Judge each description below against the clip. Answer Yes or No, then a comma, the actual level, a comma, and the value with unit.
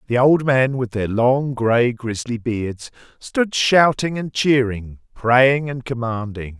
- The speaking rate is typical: Yes, average, 145 wpm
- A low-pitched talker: Yes, low, 125 Hz